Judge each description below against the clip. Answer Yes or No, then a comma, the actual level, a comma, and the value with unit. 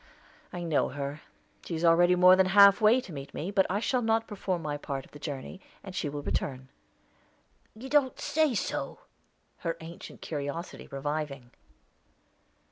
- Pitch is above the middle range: No, medium, 170 Hz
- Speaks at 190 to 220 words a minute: No, average, 165 wpm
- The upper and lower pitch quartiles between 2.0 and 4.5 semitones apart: No, wide, 5.4 semitones